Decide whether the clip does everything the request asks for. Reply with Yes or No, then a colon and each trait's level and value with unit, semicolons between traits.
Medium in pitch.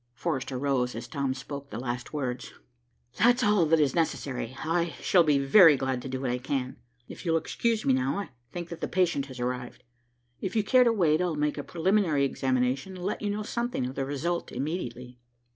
Yes: medium, 145 Hz